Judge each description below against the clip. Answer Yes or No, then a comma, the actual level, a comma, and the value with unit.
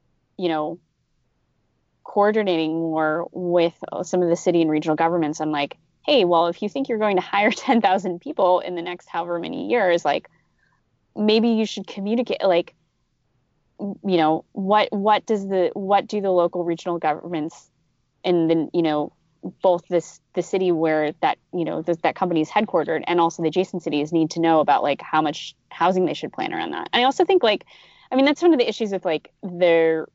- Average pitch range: Yes, average, 3.9 semitones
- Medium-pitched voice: Yes, medium, 175 Hz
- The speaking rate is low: No, average, 195 wpm